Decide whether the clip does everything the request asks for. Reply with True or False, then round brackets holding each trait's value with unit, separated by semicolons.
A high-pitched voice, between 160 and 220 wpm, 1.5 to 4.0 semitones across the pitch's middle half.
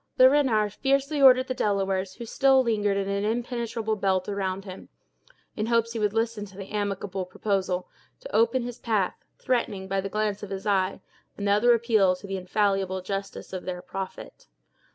True (205 Hz; 175 wpm; 3.2 semitones)